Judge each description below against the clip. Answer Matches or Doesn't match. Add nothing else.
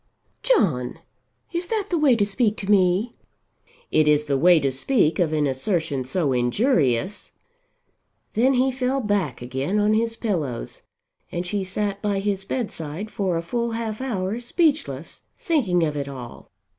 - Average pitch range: Doesn't match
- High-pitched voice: Matches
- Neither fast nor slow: Matches